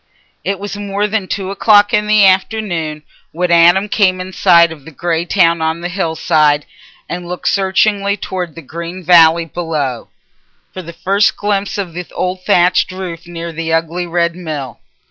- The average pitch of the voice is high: No, medium, 175 Hz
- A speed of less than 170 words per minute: No, average, 175 wpm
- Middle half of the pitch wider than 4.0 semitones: No, average, 2.9 semitones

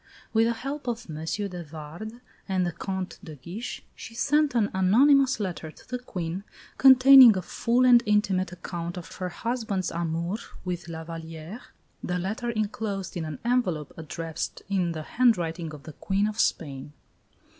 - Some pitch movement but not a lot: No, wide, 5.8 semitones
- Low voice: No, high, 190 Hz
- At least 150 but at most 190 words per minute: Yes, average, 165 wpm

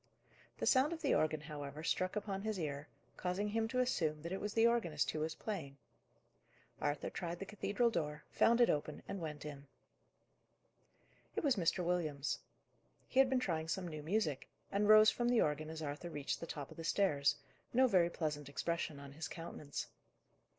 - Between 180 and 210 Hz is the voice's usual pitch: No, medium, 170 Hz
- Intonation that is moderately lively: No, wide, 5.7 semitones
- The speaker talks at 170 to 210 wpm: Yes, average, 185 wpm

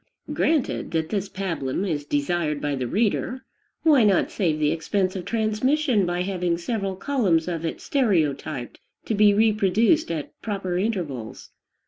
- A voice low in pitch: No, medium, 185 Hz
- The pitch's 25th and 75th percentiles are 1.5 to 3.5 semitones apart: No, average, 5.2 semitones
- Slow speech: No, average, 145 wpm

